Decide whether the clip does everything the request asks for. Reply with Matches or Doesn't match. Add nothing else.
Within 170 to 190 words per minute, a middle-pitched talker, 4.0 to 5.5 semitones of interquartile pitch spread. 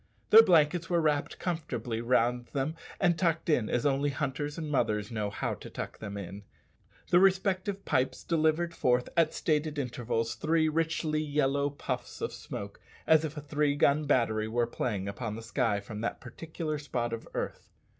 Matches